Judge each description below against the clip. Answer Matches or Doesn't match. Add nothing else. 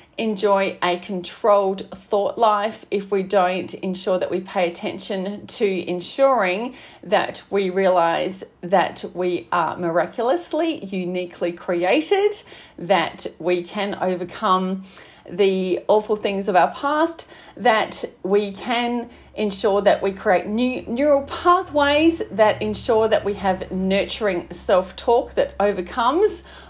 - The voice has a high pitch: Matches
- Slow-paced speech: Matches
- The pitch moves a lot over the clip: Doesn't match